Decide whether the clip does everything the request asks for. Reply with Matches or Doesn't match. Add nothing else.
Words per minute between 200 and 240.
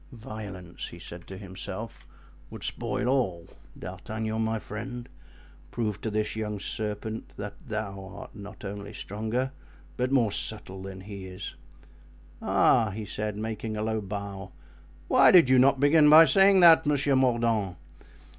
Doesn't match